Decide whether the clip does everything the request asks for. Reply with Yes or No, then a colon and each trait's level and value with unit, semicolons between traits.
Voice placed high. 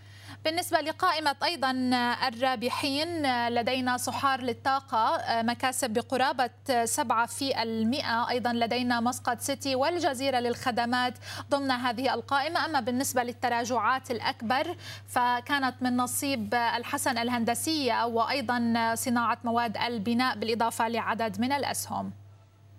Yes: very high, 250 Hz